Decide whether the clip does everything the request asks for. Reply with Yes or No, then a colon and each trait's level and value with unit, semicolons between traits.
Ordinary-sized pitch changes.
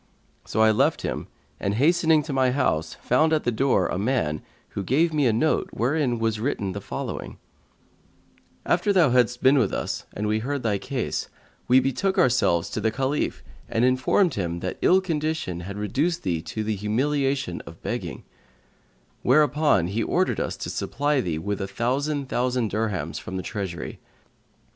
No: wide, 5.8 semitones